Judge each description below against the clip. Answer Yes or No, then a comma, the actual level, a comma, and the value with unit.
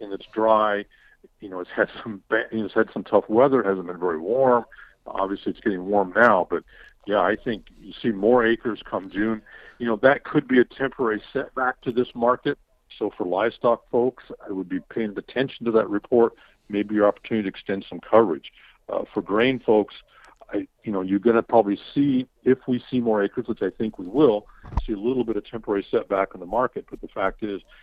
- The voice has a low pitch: Yes, low, 115 Hz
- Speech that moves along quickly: Yes, fast, 215 wpm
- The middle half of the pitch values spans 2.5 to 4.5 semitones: Yes, average, 3.6 semitones